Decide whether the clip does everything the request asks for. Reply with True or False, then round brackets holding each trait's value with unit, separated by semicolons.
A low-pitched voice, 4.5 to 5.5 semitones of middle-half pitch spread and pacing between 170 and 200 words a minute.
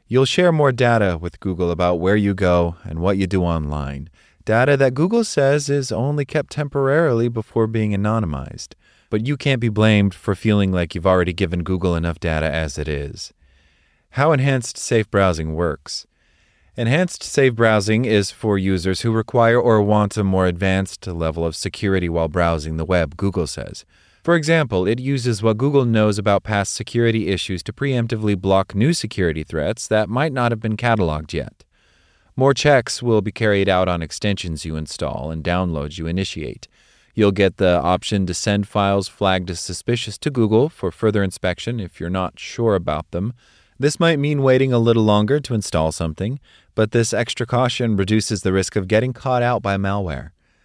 True (100 Hz; 5.0 semitones; 180 wpm)